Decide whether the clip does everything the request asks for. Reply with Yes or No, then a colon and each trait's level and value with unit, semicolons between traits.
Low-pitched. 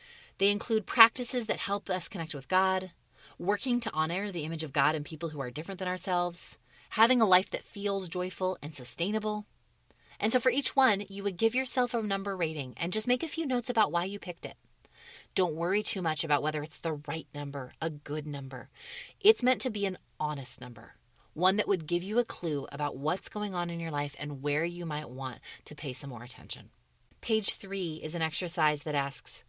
No: medium, 175 Hz